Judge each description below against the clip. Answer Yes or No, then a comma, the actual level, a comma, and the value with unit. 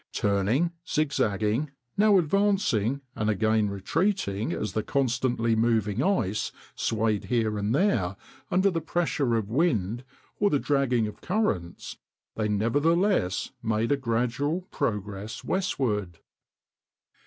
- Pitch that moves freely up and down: Yes, wide, 6.5 semitones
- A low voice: Yes, low, 115 Hz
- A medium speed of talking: No, slow, 115 wpm